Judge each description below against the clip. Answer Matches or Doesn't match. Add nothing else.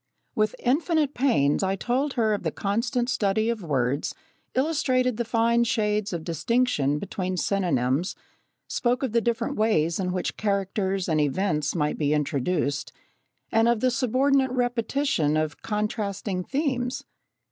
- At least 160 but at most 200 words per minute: Doesn't match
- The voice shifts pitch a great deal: Matches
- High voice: Matches